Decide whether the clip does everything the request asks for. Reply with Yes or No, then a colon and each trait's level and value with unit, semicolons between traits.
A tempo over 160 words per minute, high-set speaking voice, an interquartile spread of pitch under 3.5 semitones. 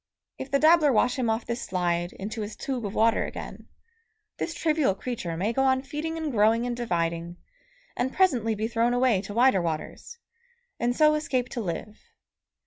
No: average, 180 wpm; high, 235 Hz; average, 4.5 semitones